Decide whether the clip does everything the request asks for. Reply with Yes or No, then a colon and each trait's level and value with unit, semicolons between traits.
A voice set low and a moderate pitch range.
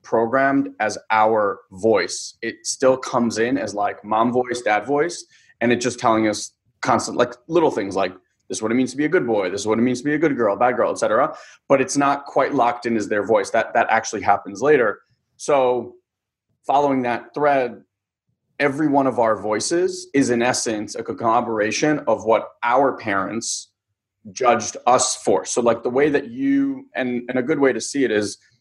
Yes: low, 120 Hz; average, 4.1 semitones